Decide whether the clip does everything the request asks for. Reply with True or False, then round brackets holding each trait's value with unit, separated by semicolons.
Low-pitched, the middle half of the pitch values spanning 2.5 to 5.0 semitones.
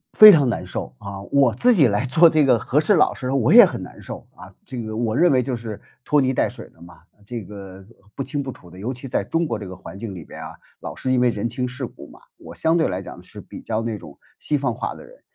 False (125 Hz; 5.6 semitones)